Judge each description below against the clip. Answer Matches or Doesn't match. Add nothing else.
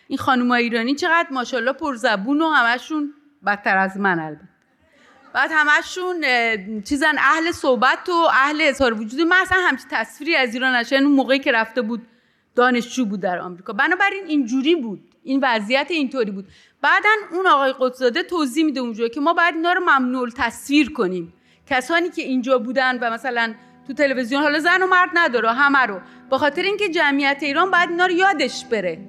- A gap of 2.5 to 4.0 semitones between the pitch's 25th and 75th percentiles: Doesn't match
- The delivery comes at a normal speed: Doesn't match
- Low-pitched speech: Doesn't match